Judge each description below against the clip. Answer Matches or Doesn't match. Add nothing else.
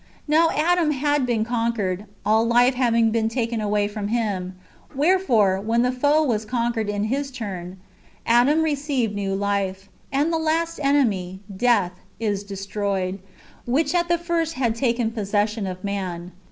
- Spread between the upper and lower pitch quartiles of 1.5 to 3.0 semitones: Doesn't match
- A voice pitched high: Matches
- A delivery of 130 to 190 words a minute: Matches